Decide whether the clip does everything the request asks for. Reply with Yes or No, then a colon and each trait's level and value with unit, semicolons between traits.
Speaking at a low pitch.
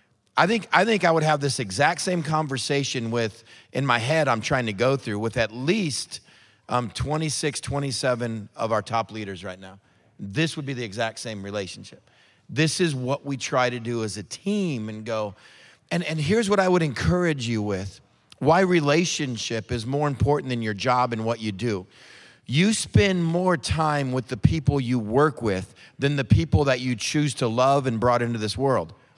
Yes: low, 130 Hz